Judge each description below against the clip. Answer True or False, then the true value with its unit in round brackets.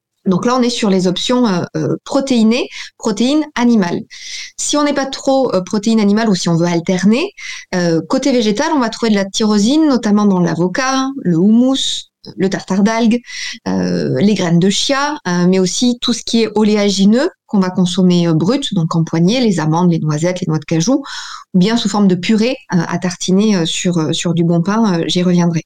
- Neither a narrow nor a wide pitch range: False (5.7 semitones)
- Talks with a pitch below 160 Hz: False (205 Hz)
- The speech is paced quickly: False (210 wpm)